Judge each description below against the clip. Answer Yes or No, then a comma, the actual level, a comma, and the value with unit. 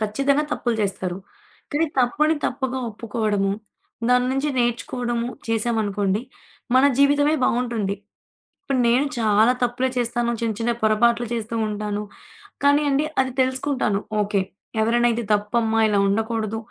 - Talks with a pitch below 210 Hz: No, high, 235 Hz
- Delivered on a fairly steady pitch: No, average, 3.2 semitones